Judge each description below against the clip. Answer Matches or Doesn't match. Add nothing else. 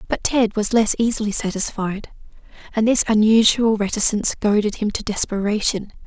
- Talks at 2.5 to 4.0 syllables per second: Doesn't match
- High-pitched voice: Matches